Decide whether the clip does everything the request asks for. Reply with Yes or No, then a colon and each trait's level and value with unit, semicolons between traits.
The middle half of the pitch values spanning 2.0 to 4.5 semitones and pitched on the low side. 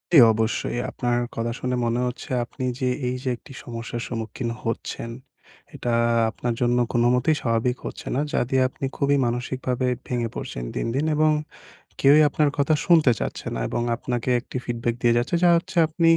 Yes: average, 2.8 semitones; low, 125 Hz